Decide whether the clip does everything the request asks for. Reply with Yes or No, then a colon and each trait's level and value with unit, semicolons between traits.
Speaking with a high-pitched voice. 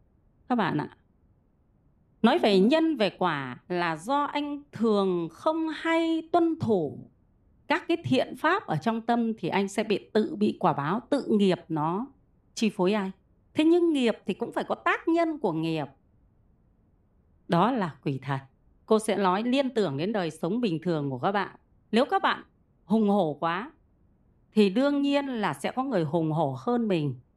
Yes: high, 205 Hz